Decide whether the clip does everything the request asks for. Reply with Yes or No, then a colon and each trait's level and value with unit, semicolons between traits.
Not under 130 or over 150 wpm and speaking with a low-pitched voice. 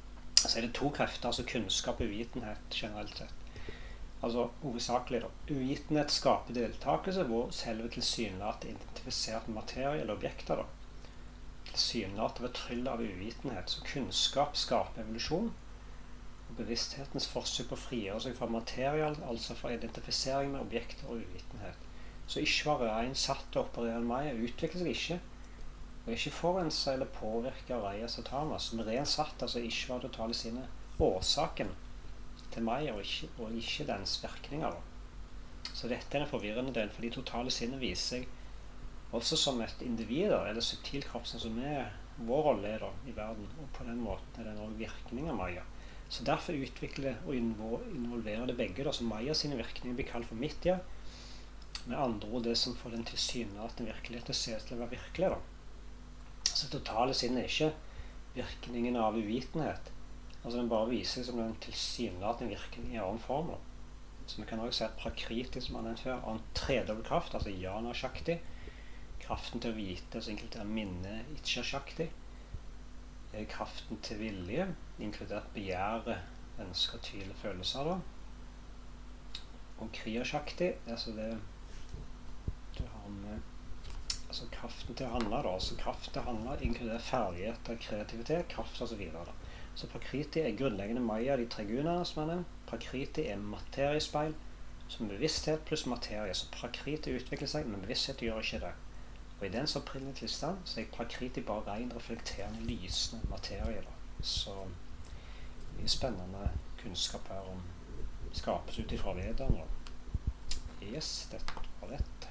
Yes: average, 145 wpm; low, 115 Hz